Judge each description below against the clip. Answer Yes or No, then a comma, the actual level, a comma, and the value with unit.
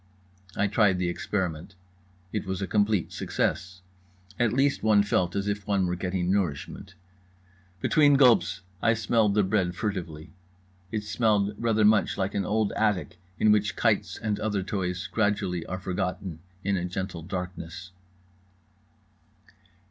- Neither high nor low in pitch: No, low, 100 Hz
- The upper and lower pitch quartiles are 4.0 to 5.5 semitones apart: No, average, 2.7 semitones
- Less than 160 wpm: Yes, average, 140 wpm